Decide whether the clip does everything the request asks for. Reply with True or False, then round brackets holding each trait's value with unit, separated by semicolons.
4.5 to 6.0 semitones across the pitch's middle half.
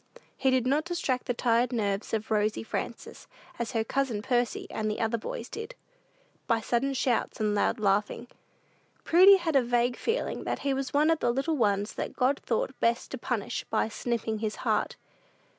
False (3.6 semitones)